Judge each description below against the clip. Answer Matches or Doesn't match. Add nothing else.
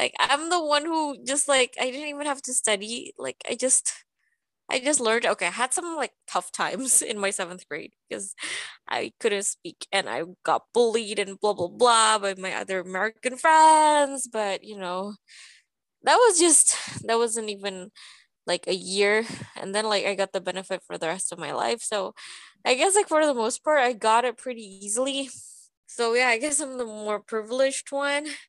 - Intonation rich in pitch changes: Matches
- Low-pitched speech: Doesn't match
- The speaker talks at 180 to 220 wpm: Matches